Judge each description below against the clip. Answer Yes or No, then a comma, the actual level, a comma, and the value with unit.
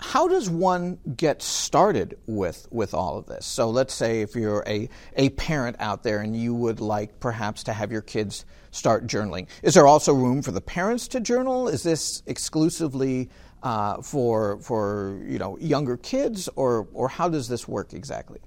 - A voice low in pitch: Yes, low, 125 Hz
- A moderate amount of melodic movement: No, wide, 7.1 semitones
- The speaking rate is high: No, average, 185 wpm